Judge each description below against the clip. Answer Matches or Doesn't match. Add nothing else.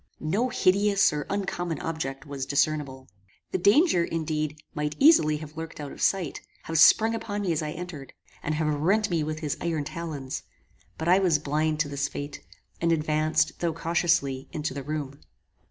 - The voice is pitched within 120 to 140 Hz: Doesn't match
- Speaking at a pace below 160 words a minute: Doesn't match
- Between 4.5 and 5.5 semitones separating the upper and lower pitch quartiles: Doesn't match